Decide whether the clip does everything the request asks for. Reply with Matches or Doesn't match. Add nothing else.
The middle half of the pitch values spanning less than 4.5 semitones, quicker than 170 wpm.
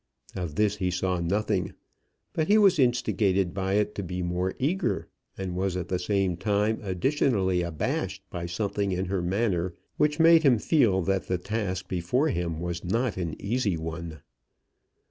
Doesn't match